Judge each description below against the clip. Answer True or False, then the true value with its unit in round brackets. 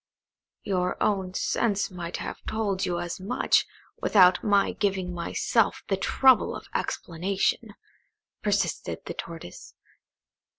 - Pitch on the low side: False (190 Hz)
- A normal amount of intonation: False (2.2 semitones)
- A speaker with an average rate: False (115 wpm)